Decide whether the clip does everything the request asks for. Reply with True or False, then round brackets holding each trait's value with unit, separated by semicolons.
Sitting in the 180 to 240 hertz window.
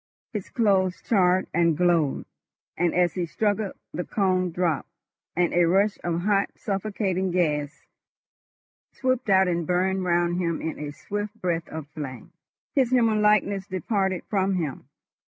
True (185 Hz)